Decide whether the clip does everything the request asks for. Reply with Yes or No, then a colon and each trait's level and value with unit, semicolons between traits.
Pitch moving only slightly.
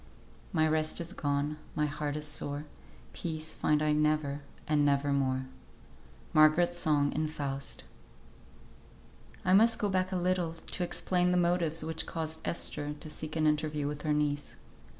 Yes: narrow, 2.3 semitones